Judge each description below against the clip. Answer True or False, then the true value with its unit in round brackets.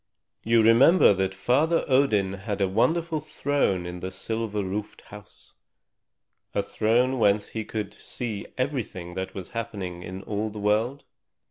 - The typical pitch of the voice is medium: False (110 Hz)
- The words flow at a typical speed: True (145 wpm)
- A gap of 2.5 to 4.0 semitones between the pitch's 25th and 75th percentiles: False (4.4 semitones)